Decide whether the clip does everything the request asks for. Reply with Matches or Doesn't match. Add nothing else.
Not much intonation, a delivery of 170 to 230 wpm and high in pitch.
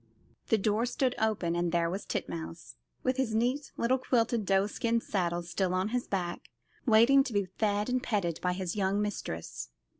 Doesn't match